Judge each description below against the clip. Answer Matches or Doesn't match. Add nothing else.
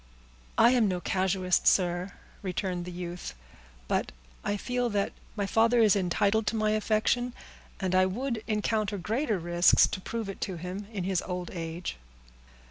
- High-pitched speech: Matches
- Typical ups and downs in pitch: Matches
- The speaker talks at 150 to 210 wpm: Matches